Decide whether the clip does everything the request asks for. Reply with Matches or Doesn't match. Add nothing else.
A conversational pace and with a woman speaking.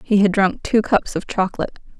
Doesn't match